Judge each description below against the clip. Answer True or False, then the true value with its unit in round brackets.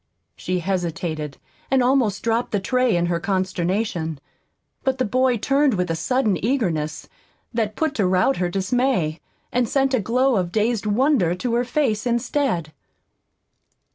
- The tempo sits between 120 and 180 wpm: True (150 wpm)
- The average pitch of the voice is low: False (215 Hz)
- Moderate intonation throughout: False (6.0 semitones)